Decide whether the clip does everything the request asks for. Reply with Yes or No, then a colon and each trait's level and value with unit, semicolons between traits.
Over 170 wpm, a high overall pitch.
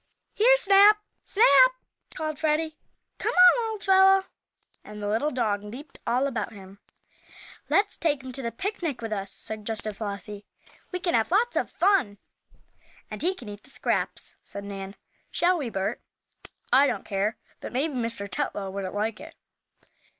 No: average, 155 wpm; very high, 255 Hz